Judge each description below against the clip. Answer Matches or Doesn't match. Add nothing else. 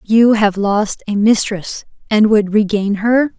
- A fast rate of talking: Doesn't match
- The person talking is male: Doesn't match